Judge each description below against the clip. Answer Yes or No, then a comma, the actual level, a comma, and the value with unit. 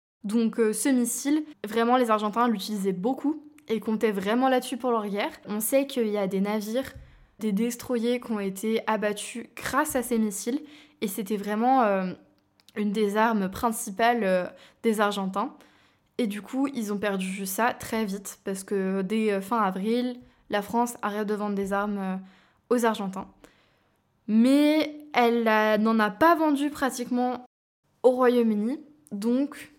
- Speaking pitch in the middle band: No, high, 225 Hz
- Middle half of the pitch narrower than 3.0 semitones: No, average, 3.3 semitones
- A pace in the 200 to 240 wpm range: No, average, 155 wpm